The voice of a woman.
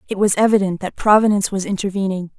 Yes: female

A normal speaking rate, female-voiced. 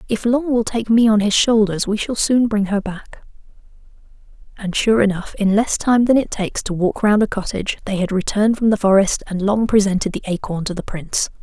No: fast, 220 wpm; female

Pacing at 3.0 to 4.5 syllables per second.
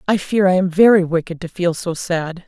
No: 5.2 syllables/s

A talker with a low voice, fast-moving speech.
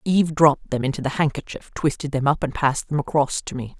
No: medium, 145 Hz; fast, 235 wpm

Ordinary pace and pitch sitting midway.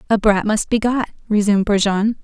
No: average, 190 wpm; high, 210 Hz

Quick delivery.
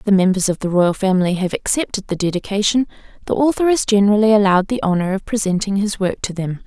Yes: fast, 215 wpm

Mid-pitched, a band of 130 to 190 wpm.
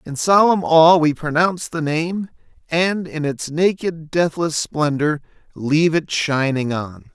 Yes: medium, 160 Hz; average, 145 wpm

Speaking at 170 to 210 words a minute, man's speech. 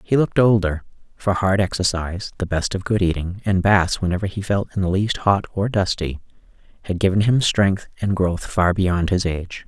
Yes: average, 200 wpm; male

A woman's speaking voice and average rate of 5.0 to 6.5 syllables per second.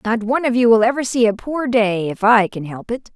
Yes: female; 5.6 syllables/s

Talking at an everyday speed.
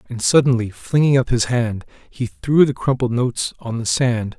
Yes: average, 190 wpm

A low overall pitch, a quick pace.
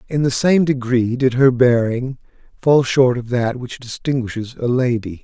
No: low, 125 Hz; average, 170 wpm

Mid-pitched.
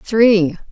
No: high, 205 Hz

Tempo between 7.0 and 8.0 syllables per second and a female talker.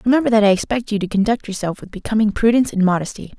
Yes: 7.4 syllables/s; female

